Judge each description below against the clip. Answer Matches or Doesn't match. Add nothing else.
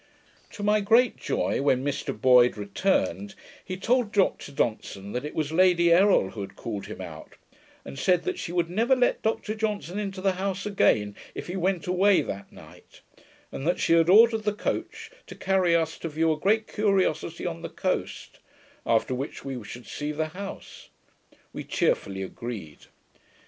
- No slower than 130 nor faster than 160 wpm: Doesn't match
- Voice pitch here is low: Doesn't match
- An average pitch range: Doesn't match